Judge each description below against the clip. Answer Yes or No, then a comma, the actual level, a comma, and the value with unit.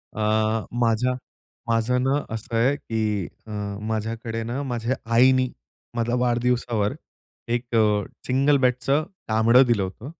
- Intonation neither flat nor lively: No, narrow, 2.3 semitones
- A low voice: Yes, low, 115 Hz